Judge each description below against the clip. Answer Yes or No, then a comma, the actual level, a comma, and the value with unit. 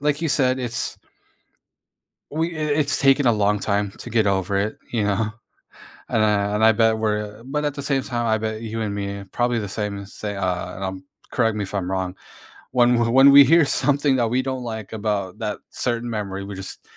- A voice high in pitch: No, low, 110 Hz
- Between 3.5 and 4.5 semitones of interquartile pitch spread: Yes, average, 3.9 semitones